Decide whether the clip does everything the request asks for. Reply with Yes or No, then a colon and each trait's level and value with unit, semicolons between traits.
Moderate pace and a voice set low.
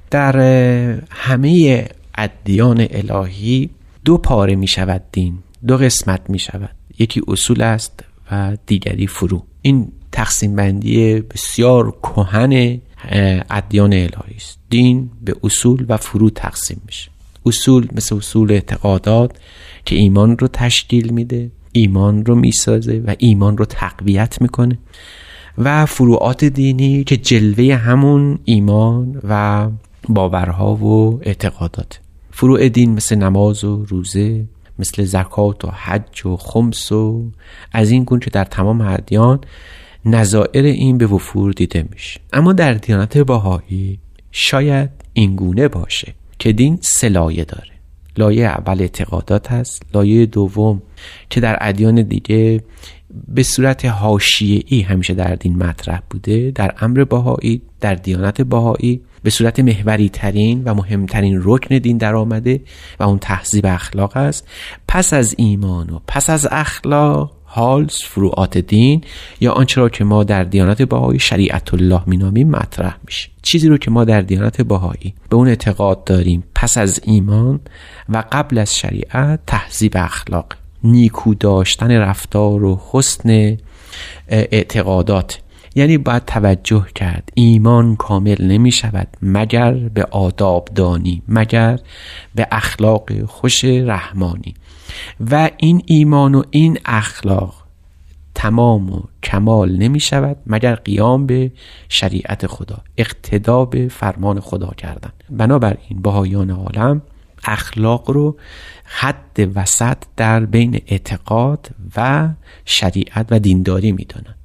Yes: average, 130 wpm; low, 105 Hz